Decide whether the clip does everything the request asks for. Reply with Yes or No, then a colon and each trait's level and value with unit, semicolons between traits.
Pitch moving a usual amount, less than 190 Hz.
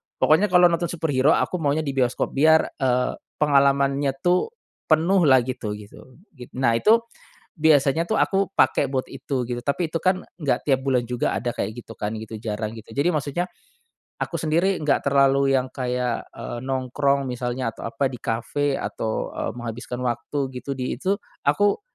Yes: average, 4.1 semitones; low, 135 Hz